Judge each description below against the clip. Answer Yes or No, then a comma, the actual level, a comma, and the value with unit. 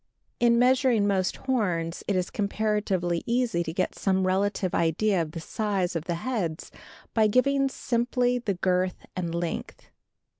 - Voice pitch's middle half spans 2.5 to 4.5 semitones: No, average, 5.1 semitones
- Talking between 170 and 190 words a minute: No, average, 150 wpm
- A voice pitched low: No, high, 200 Hz